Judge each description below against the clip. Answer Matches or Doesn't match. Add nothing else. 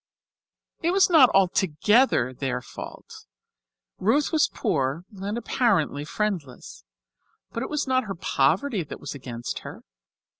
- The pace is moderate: Doesn't match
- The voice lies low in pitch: Doesn't match